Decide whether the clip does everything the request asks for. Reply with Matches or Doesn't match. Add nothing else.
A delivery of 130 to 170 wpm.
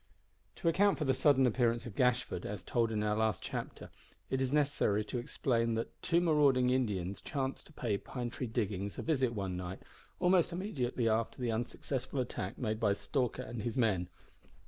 Doesn't match